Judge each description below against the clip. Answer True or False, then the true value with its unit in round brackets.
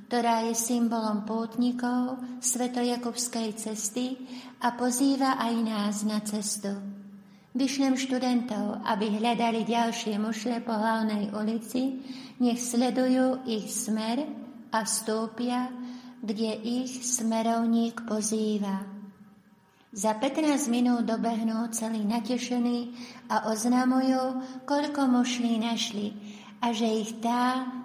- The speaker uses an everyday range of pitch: False (2.2 semitones)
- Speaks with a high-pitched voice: True (235 Hz)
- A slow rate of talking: True (100 wpm)